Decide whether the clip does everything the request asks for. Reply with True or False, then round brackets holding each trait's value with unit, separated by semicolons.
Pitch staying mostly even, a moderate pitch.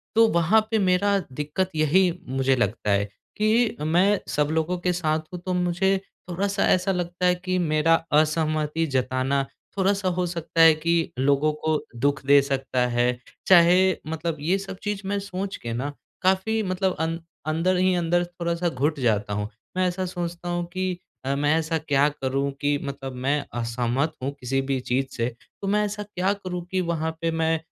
False (4.6 semitones; 165 Hz)